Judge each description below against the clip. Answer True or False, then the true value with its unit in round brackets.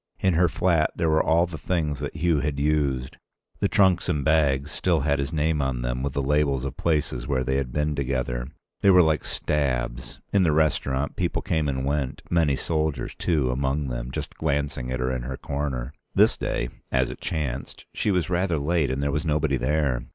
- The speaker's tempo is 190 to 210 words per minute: True (205 wpm)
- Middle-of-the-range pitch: False (70 Hz)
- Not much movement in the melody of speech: False (3.1 semitones)